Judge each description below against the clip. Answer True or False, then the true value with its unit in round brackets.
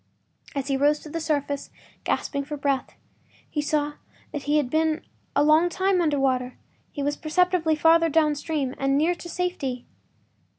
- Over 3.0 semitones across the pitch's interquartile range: False (2.5 semitones)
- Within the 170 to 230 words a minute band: False (155 wpm)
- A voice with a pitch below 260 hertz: False (295 Hz)